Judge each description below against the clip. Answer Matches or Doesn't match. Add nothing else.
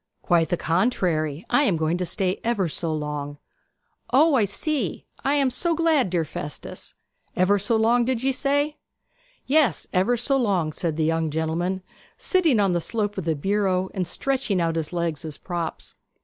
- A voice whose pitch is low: Doesn't match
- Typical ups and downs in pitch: Doesn't match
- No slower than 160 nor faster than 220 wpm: Matches